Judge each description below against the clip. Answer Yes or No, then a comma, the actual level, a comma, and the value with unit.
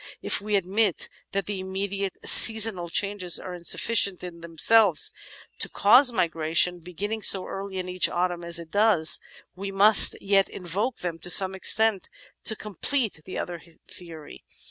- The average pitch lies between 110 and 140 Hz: No, high, 190 Hz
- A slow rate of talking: No, average, 155 wpm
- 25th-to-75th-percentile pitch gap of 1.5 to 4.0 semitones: Yes, average, 2.8 semitones